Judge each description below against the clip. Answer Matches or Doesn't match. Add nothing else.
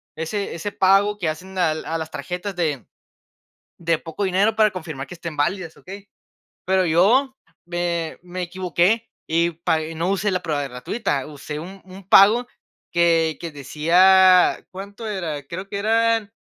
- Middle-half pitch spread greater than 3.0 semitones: Matches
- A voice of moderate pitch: Matches